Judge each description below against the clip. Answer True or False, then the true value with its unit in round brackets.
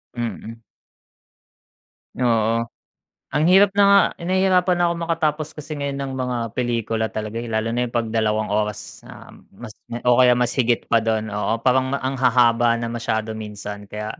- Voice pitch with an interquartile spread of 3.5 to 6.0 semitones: True (3.9 semitones)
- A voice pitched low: True (120 Hz)